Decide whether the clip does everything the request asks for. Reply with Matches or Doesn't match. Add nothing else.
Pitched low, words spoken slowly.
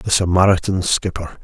Matches